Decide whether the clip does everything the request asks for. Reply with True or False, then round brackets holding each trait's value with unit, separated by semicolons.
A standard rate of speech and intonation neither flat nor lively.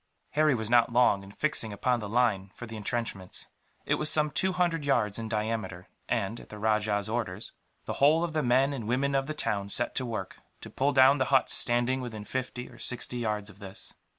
False (215 wpm; 4.2 semitones)